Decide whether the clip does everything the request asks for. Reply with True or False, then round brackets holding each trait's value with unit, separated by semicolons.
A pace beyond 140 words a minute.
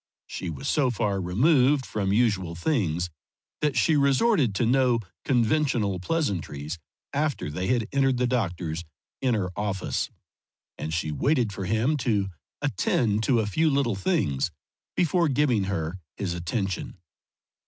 False (135 wpm)